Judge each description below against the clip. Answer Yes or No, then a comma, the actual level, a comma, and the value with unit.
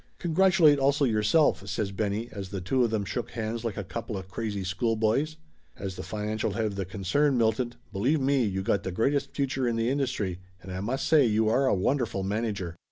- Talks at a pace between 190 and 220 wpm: Yes, fast, 205 wpm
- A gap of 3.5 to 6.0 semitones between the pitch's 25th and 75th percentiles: Yes, average, 5.1 semitones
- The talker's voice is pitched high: No, low, 110 Hz